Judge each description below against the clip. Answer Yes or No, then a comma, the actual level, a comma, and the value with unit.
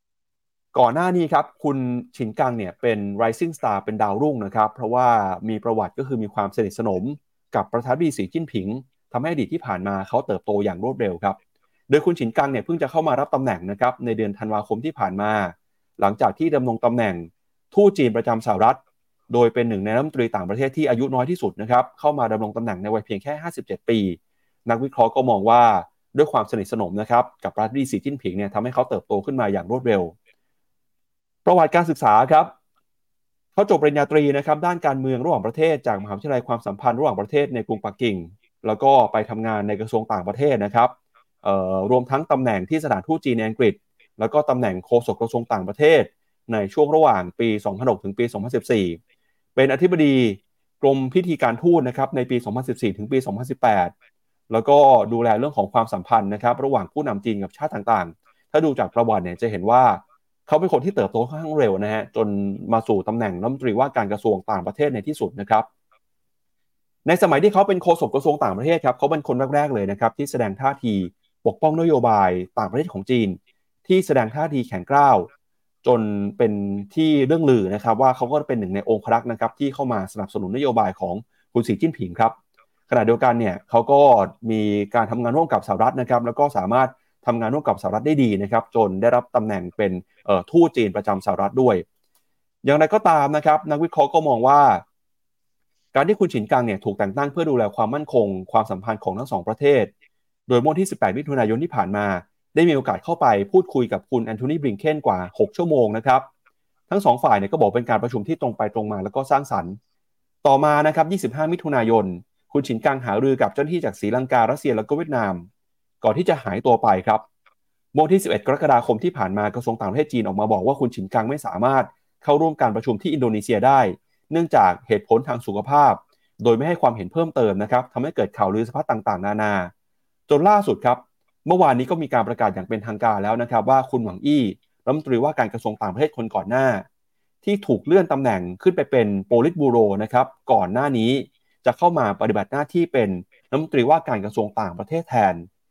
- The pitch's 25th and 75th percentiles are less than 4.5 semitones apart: No, wide, 5.5 semitones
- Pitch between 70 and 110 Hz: No, low, 120 Hz